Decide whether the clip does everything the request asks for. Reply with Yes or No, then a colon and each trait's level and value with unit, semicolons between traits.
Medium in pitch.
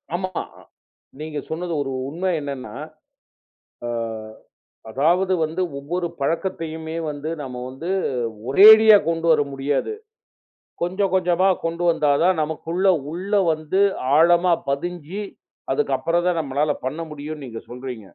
Yes: medium, 165 Hz